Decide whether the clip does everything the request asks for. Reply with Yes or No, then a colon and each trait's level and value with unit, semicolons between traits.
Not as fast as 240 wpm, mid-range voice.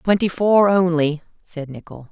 Yes: average, 140 wpm; medium, 170 Hz